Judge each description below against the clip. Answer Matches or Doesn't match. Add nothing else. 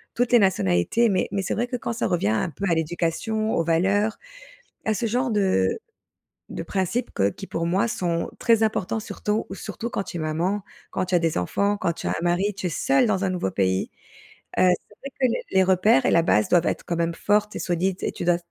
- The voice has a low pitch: Doesn't match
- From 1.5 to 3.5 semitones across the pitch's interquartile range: Doesn't match